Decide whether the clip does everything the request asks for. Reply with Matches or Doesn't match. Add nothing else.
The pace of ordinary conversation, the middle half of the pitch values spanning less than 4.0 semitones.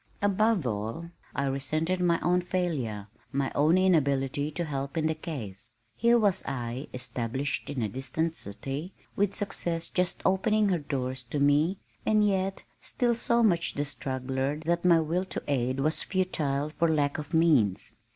Doesn't match